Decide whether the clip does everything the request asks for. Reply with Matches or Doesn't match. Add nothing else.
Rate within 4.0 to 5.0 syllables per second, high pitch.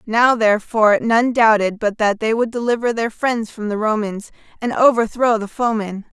Matches